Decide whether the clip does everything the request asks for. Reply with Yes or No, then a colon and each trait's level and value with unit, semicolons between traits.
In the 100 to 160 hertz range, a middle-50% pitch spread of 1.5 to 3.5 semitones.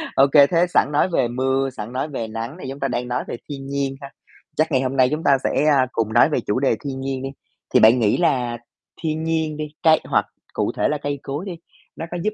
Yes: low, 135 Hz; average, 3.1 semitones